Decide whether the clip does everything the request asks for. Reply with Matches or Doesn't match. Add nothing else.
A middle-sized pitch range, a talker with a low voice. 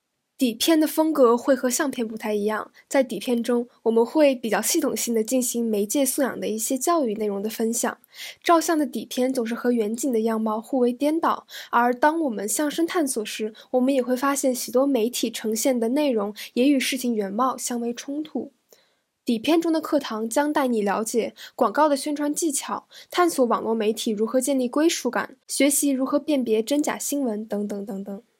Doesn't match